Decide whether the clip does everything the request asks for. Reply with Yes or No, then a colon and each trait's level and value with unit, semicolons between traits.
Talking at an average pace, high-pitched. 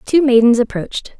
Yes: average, 150 wpm; high, 245 Hz